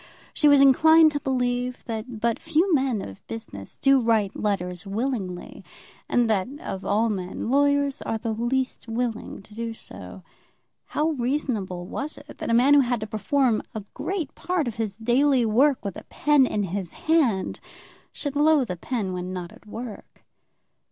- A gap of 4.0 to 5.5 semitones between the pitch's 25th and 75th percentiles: Yes, average, 4.9 semitones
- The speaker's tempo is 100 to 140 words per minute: No, average, 170 wpm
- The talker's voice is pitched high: Yes, high, 240 Hz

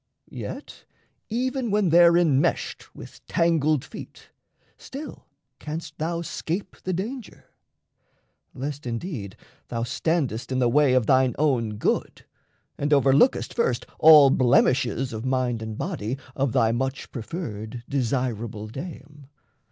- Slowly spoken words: Yes, slow, 120 wpm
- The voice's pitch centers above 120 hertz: Yes, low, 135 Hz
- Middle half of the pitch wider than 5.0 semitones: Yes, wide, 5.6 semitones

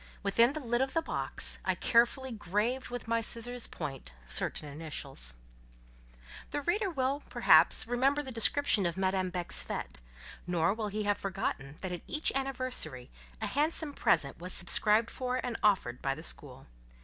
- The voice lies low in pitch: No, high, 220 Hz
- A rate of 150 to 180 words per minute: Yes, average, 160 wpm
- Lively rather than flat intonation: Yes, wide, 6.9 semitones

